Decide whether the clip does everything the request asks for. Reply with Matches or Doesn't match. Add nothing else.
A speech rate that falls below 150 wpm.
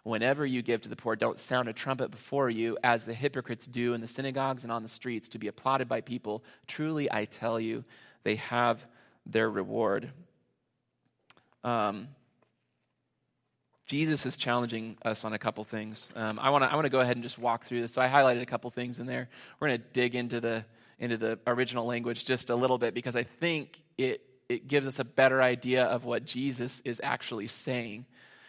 Doesn't match